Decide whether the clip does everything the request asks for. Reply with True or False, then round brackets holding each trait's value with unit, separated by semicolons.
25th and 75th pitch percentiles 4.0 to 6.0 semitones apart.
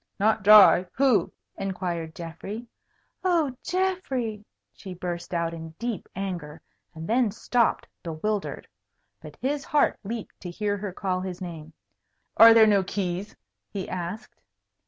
True (4.5 semitones)